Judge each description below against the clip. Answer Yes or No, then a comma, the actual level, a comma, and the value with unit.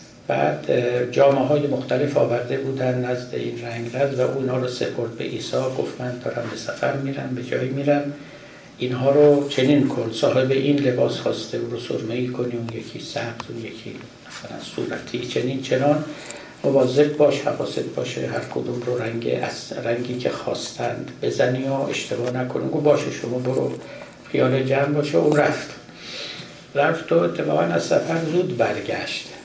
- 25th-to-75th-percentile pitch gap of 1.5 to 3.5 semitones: Yes, average, 2.7 semitones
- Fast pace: Yes, fast, 160 wpm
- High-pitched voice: No, low, 135 Hz